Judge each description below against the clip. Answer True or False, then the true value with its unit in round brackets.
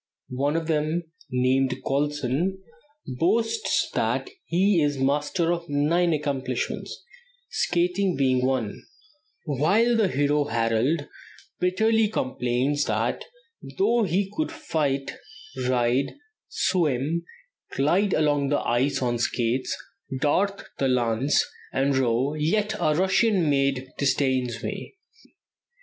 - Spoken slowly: True (105 wpm)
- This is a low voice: False (145 Hz)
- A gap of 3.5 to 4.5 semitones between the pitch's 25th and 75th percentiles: False (5.2 semitones)